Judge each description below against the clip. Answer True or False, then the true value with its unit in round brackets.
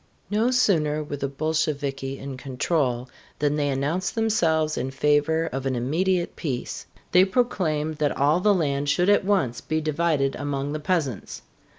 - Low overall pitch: False (150 Hz)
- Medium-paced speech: True (160 wpm)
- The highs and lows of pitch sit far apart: False (3.9 semitones)